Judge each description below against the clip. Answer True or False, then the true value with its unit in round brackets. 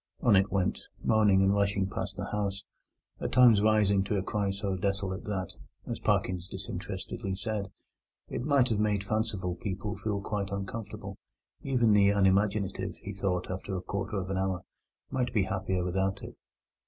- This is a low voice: True (100 Hz)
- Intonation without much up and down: True (1.8 semitones)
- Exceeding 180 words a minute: False (165 wpm)